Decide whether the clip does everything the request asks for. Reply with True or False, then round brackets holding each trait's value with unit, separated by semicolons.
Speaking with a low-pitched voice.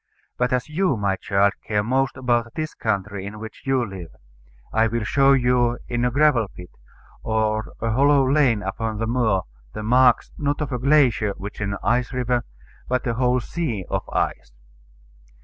True (120 Hz)